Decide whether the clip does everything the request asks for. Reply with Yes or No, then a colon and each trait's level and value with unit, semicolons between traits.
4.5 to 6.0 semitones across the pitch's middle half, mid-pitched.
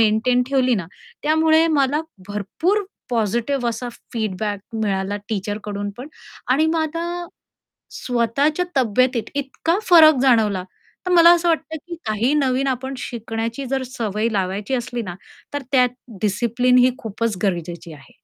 No: average, 4.9 semitones; high, 245 Hz